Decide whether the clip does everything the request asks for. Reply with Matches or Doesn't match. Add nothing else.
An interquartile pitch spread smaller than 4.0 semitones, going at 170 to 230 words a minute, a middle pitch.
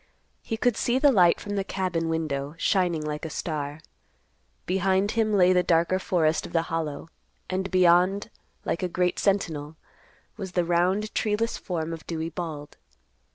Doesn't match